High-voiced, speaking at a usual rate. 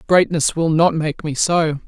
No: medium, 160 Hz; average, 190 wpm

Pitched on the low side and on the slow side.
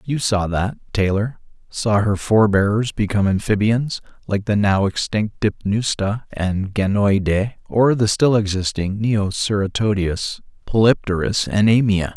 Yes: low, 105 Hz; slow, 115 wpm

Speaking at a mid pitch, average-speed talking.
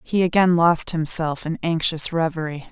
Yes: medium, 165 Hz; average, 155 wpm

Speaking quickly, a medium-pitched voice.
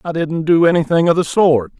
Yes: fast, 235 wpm; medium, 160 Hz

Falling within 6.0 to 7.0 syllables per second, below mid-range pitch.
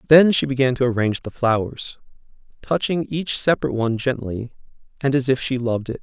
Yes: 6.1 syllables/s; low, 130 Hz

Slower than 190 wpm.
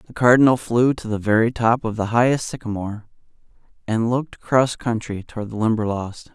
Yes: average, 170 wpm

